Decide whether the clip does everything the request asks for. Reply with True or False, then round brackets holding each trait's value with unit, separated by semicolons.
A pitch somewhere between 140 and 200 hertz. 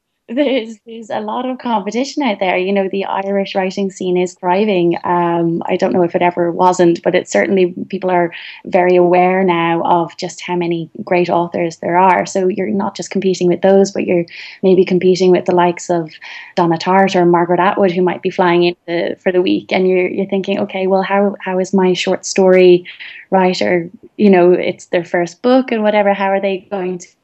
True (185 Hz)